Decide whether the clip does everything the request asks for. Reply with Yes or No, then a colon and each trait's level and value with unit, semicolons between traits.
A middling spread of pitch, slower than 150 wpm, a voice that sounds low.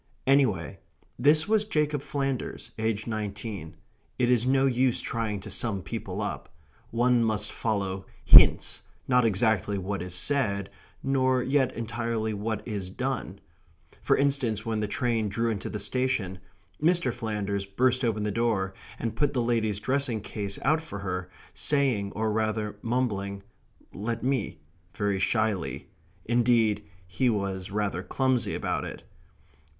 Yes: average, 3.9 semitones; average, 140 wpm; low, 110 Hz